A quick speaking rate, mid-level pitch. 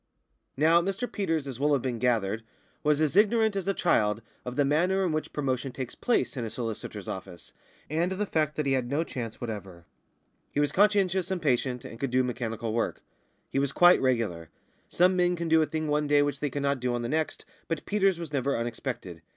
Yes: fast, 215 wpm; medium, 145 Hz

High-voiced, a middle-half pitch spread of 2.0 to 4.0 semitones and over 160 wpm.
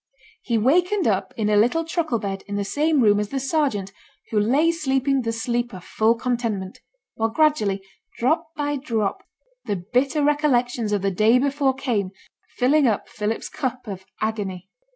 No: high, 240 Hz; average, 5.3 semitones; average, 170 wpm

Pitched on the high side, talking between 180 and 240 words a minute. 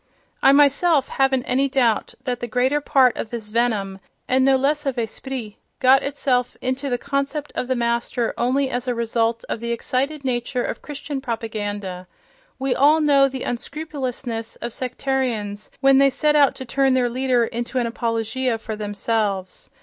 No: very high, 250 Hz; average, 170 wpm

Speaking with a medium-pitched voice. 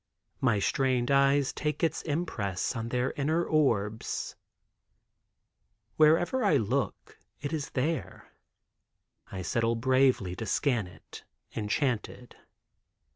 No: low, 130 Hz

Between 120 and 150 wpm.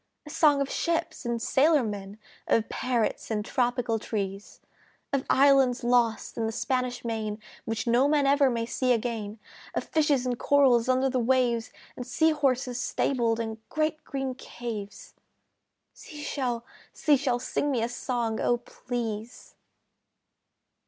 Yes: average, 145 wpm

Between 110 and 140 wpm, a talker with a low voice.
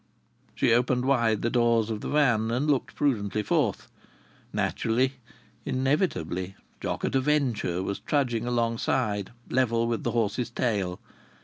Yes: slow, 135 wpm; low, 120 Hz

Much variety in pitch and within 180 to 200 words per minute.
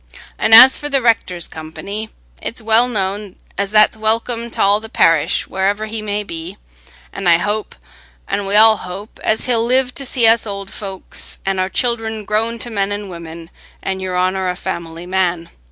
No: average, 3.2 semitones; average, 185 wpm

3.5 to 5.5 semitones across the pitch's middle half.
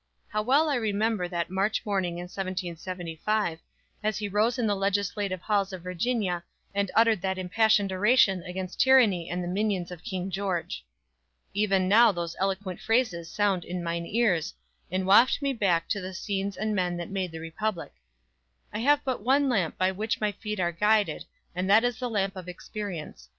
No: average, 3.1 semitones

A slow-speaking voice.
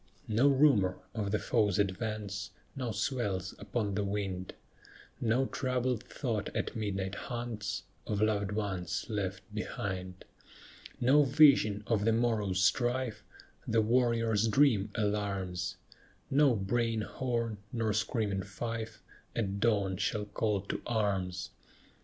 Yes: slow, 120 wpm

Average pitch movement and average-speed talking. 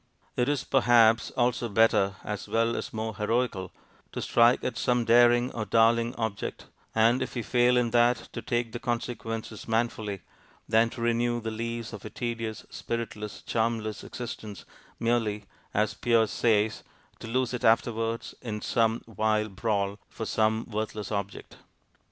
No: narrow, 1.6 semitones; average, 150 wpm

